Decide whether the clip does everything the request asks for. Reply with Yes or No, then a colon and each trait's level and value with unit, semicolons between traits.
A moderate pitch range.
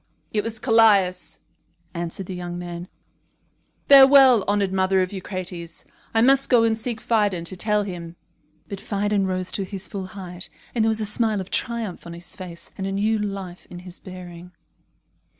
Yes: average, 3.3 semitones